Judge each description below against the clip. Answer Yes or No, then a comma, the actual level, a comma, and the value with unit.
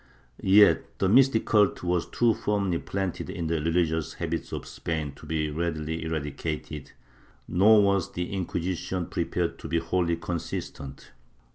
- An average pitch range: Yes, average, 3.0 semitones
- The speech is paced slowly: No, average, 145 wpm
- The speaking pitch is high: No, very low, 85 Hz